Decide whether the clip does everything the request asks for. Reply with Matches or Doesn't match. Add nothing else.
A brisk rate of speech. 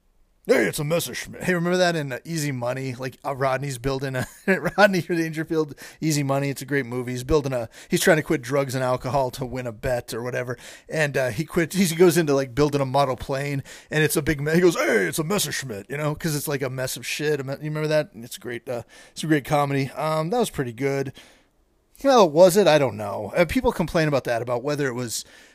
Matches